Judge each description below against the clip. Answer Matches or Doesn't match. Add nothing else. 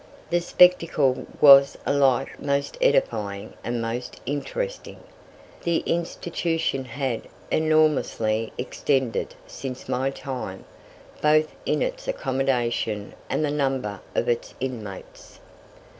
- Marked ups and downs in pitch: Doesn't match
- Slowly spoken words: Matches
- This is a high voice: Doesn't match